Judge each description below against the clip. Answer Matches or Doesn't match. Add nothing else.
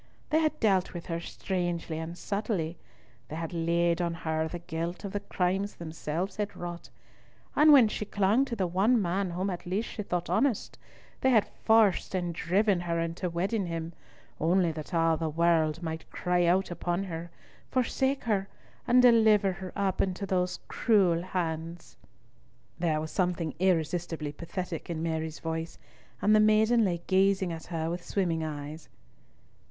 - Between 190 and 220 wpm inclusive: Doesn't match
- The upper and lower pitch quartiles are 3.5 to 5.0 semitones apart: Doesn't match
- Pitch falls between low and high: Matches